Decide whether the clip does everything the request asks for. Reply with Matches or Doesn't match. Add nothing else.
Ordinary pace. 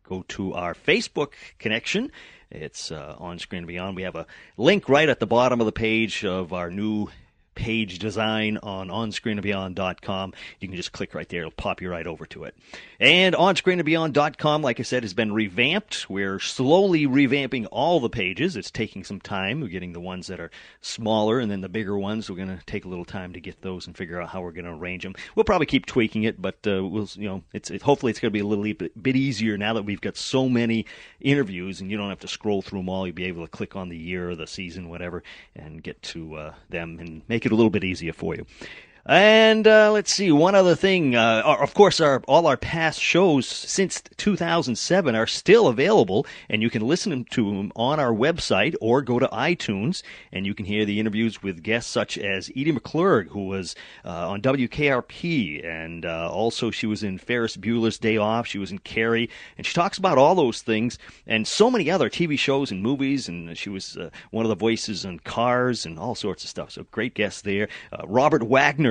Doesn't match